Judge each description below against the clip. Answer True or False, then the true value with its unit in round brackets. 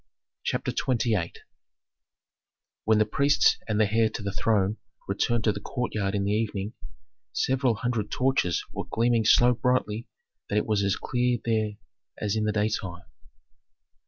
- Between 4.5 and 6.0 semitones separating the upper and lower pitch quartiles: False (2.7 semitones)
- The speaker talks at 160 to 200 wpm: False (150 wpm)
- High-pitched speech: False (110 Hz)